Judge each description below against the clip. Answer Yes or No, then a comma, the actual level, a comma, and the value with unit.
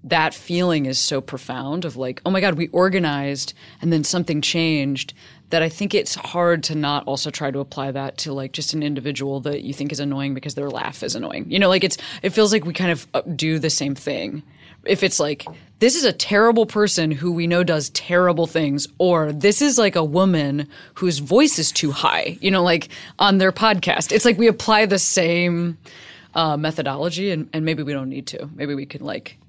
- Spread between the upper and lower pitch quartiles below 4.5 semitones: Yes, average, 3.9 semitones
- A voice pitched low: No, medium, 160 Hz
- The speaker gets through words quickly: Yes, fast, 220 wpm